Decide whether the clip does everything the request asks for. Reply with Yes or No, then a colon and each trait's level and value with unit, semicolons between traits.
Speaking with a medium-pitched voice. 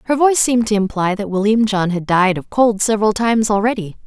No: high, 210 Hz